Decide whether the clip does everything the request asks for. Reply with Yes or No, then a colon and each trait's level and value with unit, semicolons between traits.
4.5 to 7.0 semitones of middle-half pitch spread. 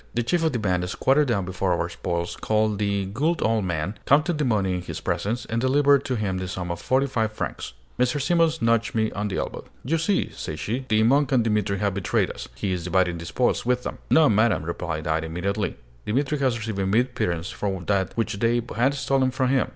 Yes: wide, 5.6 semitones